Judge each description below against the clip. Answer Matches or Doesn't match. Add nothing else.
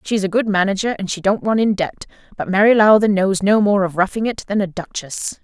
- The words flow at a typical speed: Doesn't match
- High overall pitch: Matches